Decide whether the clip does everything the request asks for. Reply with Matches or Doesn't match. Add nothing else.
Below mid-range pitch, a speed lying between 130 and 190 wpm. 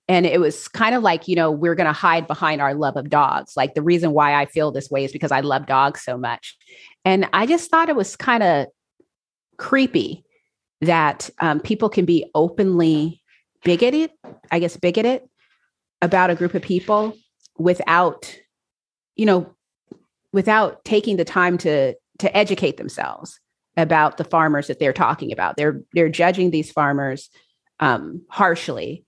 Doesn't match